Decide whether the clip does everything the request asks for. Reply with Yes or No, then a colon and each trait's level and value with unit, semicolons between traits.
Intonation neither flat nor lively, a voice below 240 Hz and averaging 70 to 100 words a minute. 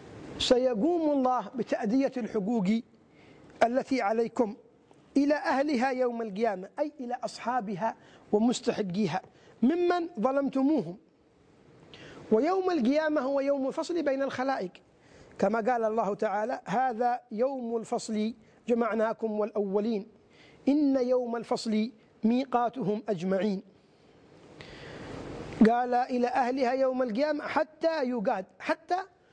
No: average, 3.8 semitones; high, 245 Hz; average, 90 wpm